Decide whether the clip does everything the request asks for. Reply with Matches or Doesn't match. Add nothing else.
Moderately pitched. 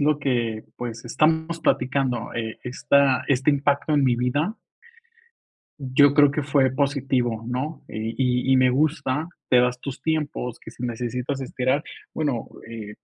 Doesn't match